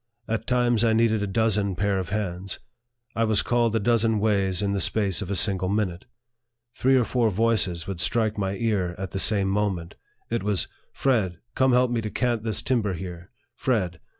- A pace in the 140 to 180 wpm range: No, average, 200 wpm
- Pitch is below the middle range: Yes, low, 105 Hz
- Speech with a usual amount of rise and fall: Yes, average, 3.1 semitones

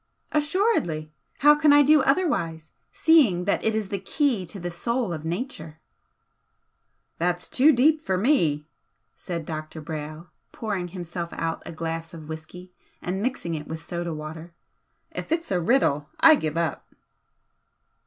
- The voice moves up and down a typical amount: No, wide, 8.4 semitones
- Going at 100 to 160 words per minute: Yes, average, 155 wpm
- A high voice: No, medium, 175 Hz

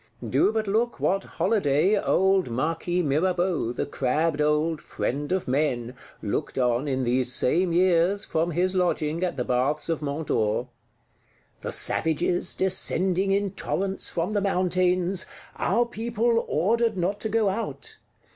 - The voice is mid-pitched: Yes, medium, 175 Hz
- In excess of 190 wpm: No, average, 145 wpm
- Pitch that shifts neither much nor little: Yes, average, 4.7 semitones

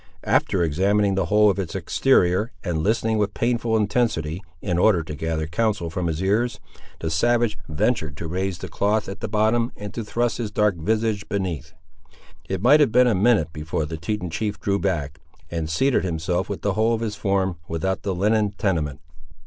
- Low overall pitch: Yes, low, 100 Hz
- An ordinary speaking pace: Yes, average, 190 wpm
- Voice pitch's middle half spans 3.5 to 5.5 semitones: Yes, average, 4.7 semitones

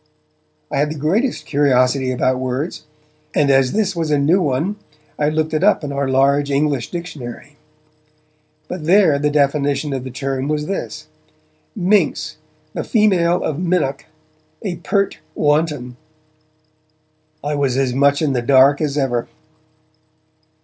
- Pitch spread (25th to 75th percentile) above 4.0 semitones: No, average, 3.4 semitones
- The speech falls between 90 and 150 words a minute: Yes, average, 145 wpm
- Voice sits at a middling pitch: Yes, medium, 145 Hz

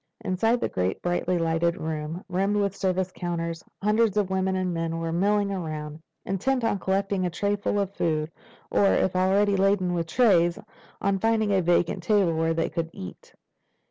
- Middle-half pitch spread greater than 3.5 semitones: No, average, 3.1 semitones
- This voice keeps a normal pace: Yes, average, 175 wpm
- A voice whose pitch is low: No, medium, 185 Hz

